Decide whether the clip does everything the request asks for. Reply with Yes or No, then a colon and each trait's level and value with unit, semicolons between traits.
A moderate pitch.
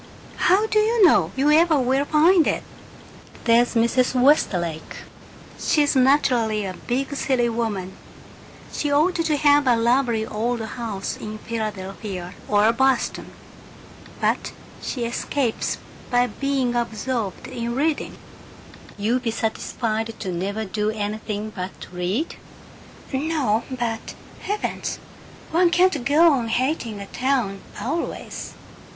No: high, 240 Hz